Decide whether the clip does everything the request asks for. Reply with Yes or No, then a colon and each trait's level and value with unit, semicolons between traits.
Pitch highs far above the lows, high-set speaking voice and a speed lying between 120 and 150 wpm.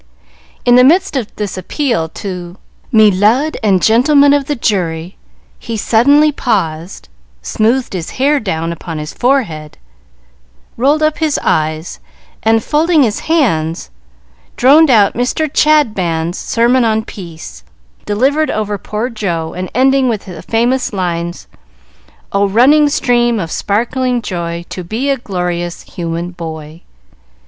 Yes: wide, 7.1 semitones; high, 215 Hz; slow, 135 wpm